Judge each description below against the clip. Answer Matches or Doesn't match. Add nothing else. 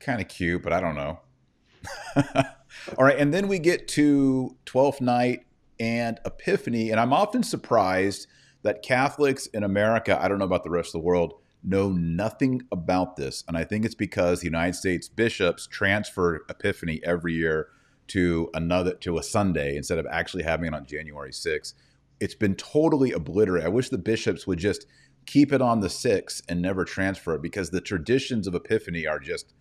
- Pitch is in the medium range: Doesn't match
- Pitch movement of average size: Doesn't match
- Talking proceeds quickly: Doesn't match